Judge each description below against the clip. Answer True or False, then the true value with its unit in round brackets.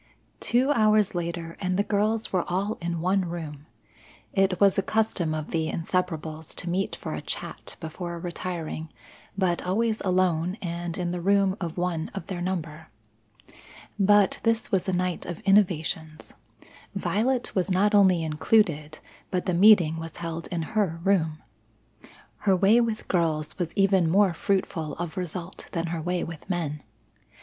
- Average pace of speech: True (160 wpm)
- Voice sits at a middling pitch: True (180 Hz)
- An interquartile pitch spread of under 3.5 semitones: True (3.0 semitones)